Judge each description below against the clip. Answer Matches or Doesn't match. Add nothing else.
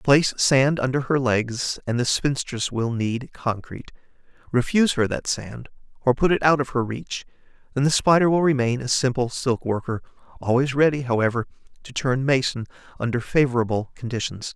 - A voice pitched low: Matches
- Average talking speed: Matches